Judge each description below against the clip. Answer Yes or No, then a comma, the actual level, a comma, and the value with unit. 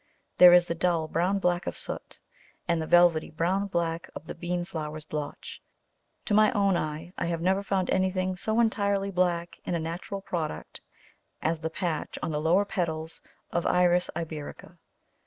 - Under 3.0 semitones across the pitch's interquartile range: Yes, narrow, 2.5 semitones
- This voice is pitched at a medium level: Yes, medium, 175 Hz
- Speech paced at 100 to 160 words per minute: No, average, 175 wpm